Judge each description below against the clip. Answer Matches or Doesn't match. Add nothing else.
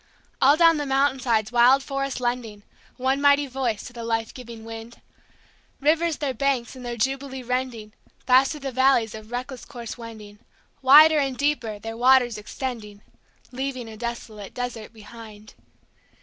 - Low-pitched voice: Doesn't match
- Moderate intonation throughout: Matches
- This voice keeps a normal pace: Matches